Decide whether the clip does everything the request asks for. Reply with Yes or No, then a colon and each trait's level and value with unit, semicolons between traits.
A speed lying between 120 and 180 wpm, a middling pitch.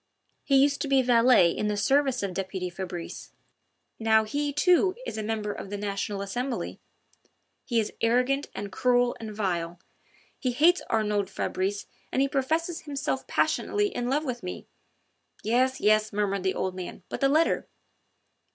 No: average, 160 wpm; high, 230 Hz